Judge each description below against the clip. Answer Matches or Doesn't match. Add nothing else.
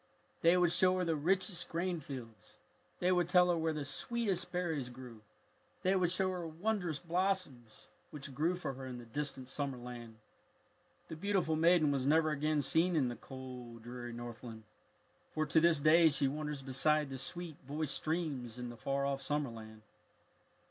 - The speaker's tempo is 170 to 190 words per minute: Matches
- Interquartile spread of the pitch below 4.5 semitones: Doesn't match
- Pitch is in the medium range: Matches